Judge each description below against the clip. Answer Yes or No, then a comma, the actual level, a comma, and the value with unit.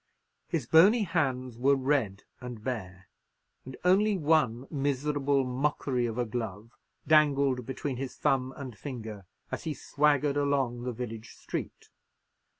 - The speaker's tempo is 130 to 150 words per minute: Yes, slow, 135 wpm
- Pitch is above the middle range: No, low, 130 Hz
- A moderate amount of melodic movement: Yes, average, 3.3 semitones